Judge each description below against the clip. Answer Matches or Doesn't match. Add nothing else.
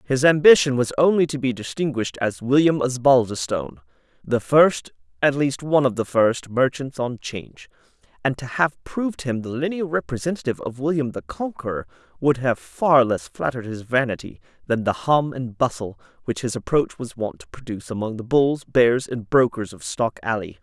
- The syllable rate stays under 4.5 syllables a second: Doesn't match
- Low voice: Matches